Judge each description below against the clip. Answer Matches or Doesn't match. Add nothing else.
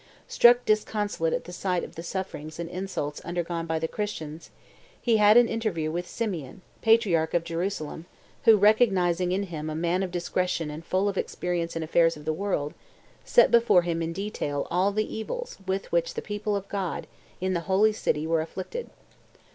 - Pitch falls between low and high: Matches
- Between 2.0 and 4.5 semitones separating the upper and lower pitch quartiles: Matches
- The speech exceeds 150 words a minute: Matches